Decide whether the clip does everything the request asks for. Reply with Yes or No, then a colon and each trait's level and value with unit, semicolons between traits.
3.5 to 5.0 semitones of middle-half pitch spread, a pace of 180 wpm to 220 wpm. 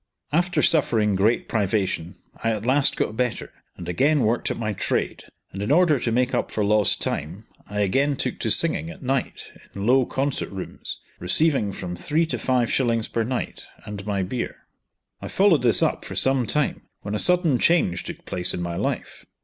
No: wide, 5.4 semitones; average, 190 wpm